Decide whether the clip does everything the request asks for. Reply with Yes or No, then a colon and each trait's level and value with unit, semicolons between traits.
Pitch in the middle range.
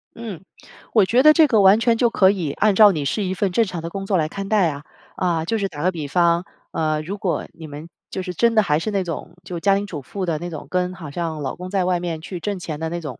Yes: medium, 180 Hz